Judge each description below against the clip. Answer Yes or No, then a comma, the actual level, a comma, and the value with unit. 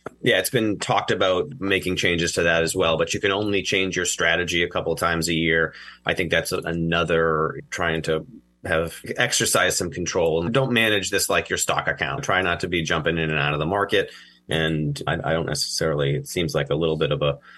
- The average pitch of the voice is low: Yes, very low, 85 Hz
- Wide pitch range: No, narrow, 2.4 semitones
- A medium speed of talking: No, fast, 225 wpm